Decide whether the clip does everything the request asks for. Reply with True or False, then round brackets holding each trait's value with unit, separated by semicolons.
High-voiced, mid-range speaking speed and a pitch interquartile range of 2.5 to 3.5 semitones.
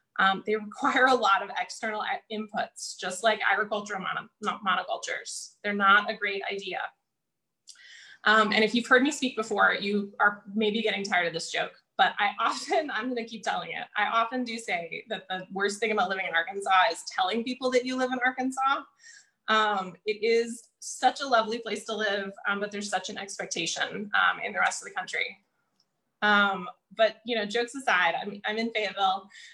True (215 Hz; 195 wpm; 3.0 semitones)